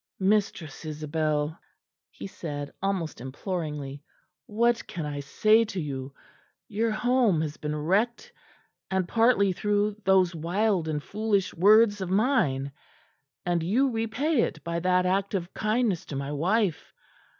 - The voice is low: No, medium, 185 Hz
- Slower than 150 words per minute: Yes, slow, 135 wpm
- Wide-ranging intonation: Yes, wide, 5.7 semitones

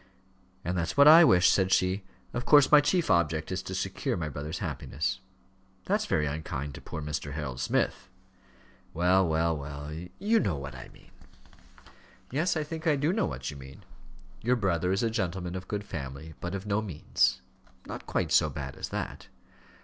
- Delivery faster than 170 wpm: Yes, average, 185 wpm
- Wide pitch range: Yes, wide, 6.3 semitones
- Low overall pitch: Yes, very low, 90 Hz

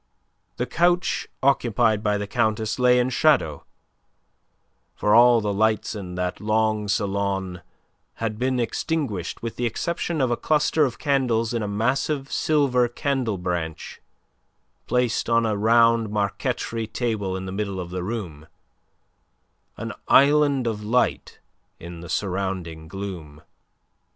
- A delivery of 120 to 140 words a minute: Yes, slow, 135 wpm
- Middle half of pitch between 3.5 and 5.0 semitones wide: Yes, average, 4.1 semitones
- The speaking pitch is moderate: No, low, 110 Hz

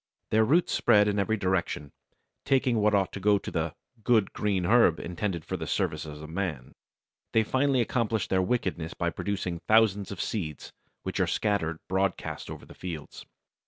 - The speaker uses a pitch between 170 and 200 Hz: No, low, 100 Hz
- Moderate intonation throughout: Yes, average, 4.2 semitones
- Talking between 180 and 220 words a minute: No, average, 170 wpm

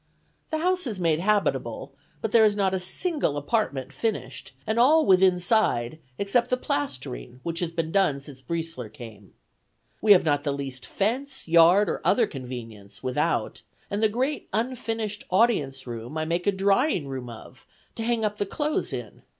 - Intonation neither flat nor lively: No, wide, 8.3 semitones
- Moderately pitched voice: Yes, medium, 180 Hz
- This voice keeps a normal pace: Yes, average, 165 wpm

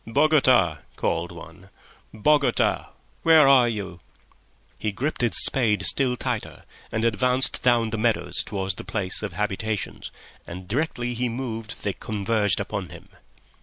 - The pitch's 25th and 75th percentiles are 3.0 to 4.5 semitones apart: Yes, average, 3.6 semitones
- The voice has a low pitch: Yes, low, 115 Hz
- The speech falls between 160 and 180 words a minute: No, slow, 135 wpm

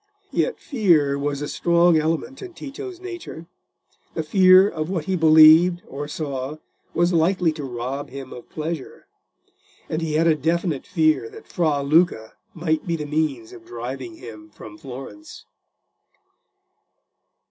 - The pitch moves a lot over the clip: No, average, 4.0 semitones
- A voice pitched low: No, medium, 155 Hz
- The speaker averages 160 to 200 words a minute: No, average, 140 wpm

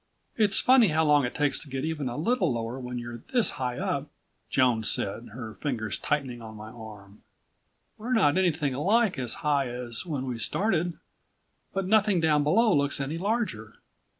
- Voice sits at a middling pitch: Yes, medium, 145 Hz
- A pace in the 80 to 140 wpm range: No, average, 180 wpm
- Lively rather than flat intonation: Yes, wide, 6.8 semitones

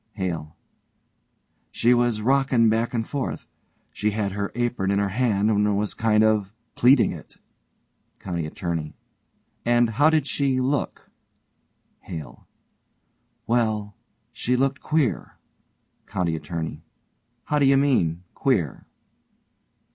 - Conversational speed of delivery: No, slow, 115 wpm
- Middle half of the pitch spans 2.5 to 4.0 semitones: No, average, 4.5 semitones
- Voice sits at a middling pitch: No, low, 110 Hz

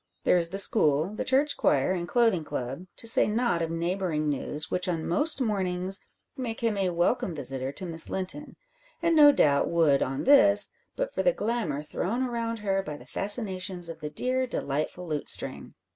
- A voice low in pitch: No, medium, 185 Hz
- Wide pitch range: Yes, wide, 6.3 semitones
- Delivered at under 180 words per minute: No, average, 185 wpm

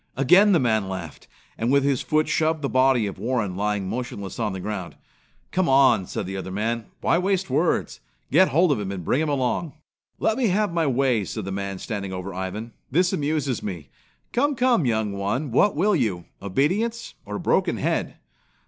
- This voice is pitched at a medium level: No, low, 125 Hz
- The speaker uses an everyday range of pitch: No, wide, 8.1 semitones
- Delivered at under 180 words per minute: No, average, 195 wpm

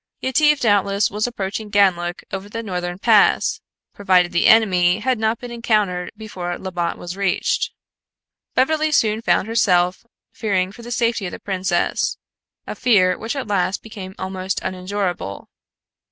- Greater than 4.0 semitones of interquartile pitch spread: No, average, 3.6 semitones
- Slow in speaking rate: No, average, 145 wpm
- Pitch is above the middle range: Yes, high, 200 Hz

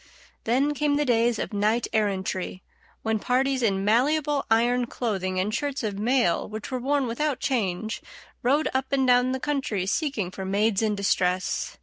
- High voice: Yes, high, 235 Hz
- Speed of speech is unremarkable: Yes, average, 165 wpm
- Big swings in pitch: No, average, 4.7 semitones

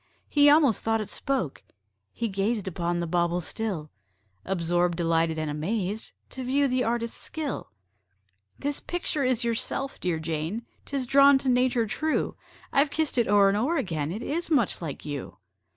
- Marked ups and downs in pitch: Yes, wide, 7.8 semitones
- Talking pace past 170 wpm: No, average, 165 wpm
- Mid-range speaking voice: No, high, 225 Hz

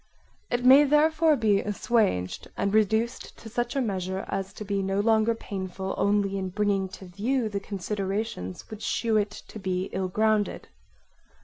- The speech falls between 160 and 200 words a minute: Yes, average, 165 wpm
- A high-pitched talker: Yes, high, 205 Hz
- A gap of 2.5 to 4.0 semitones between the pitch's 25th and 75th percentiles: Yes, average, 2.8 semitones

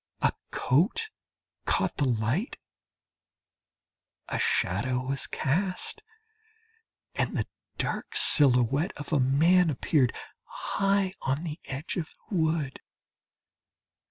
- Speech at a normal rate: No, slow, 100 wpm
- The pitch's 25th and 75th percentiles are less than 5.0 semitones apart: No, average, 5.3 semitones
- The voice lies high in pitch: No, medium, 150 Hz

